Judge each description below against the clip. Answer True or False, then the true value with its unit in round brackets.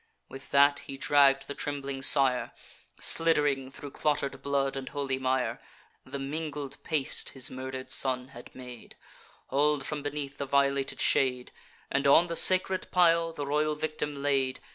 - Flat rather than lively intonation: True (1.7 semitones)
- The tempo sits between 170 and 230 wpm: False (150 wpm)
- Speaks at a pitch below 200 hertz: True (140 Hz)